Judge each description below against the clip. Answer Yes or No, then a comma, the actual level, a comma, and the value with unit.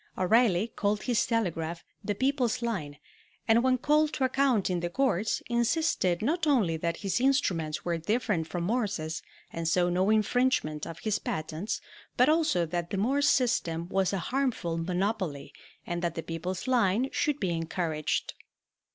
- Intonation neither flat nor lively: No, wide, 6.5 semitones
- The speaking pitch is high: Yes, high, 195 Hz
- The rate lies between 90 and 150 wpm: No, average, 160 wpm